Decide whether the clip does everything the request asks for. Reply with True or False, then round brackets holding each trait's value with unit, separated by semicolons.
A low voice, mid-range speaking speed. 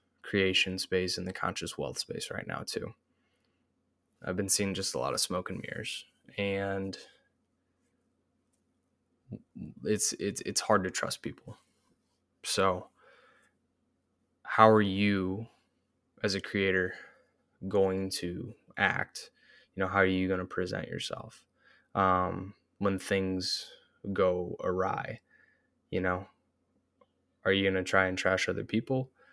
False (95 Hz; 125 wpm)